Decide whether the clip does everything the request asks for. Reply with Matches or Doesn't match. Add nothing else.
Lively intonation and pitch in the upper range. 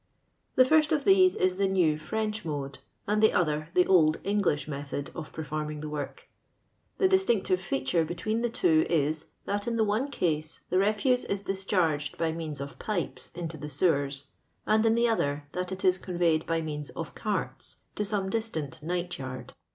Doesn't match